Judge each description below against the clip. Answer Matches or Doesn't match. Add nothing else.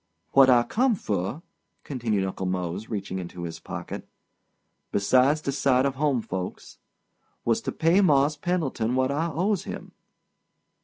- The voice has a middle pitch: Doesn't match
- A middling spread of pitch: Doesn't match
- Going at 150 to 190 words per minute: Doesn't match